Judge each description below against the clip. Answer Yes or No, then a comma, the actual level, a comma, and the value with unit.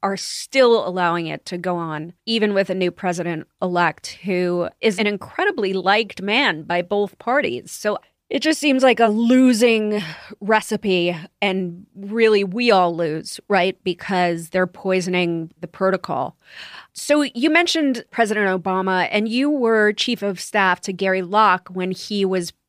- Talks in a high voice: Yes, high, 195 Hz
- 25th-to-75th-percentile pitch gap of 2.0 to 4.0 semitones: Yes, average, 3.5 semitones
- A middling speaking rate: Yes, average, 150 wpm